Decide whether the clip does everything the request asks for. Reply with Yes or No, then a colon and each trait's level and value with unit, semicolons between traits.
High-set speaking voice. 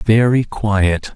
No: low, 110 Hz